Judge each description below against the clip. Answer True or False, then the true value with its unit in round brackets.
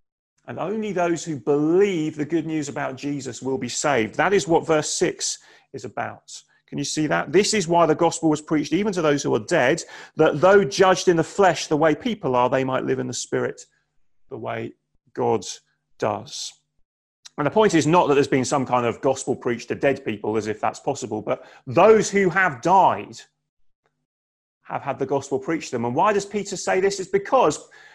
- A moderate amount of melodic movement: False (5.9 semitones)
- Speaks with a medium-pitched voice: True (160 Hz)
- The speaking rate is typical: False (210 wpm)